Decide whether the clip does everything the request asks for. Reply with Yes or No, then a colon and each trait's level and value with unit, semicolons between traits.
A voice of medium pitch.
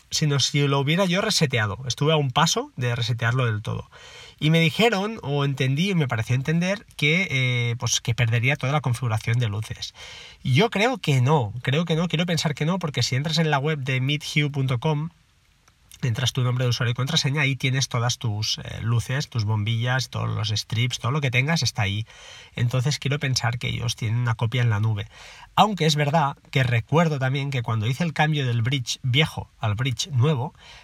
No: low, 130 Hz